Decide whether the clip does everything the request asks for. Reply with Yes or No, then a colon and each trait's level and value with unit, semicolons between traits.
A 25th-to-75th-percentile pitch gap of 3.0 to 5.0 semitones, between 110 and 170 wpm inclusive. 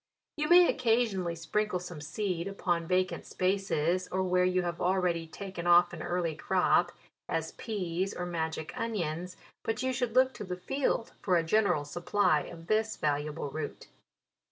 Yes: average, 3.5 semitones; average, 165 wpm